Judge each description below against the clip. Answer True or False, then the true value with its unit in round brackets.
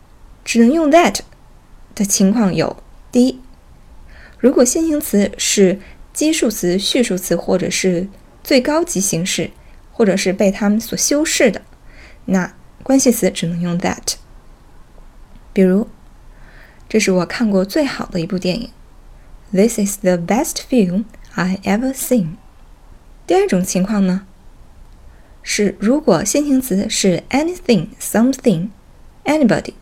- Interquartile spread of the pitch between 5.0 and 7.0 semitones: True (5.3 semitones)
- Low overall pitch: False (205 Hz)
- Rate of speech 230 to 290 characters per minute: True (265 characters per minute)